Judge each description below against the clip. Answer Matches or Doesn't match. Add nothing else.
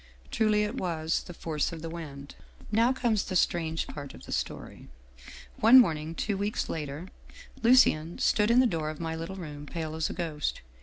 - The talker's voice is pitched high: Doesn't match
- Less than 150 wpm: Doesn't match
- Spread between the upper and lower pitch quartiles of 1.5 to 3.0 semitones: Doesn't match